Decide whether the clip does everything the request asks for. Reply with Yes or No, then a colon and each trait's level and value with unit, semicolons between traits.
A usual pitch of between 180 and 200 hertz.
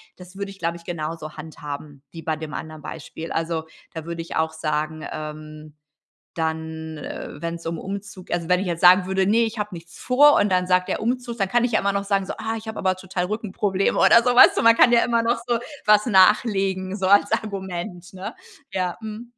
Yes: medium, 185 Hz